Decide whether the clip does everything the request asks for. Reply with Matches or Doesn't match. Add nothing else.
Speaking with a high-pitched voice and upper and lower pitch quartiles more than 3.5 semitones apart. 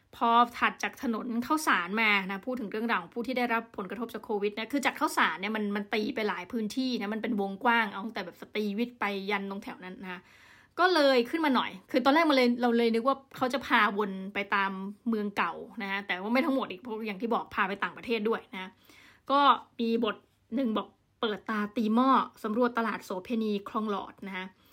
Doesn't match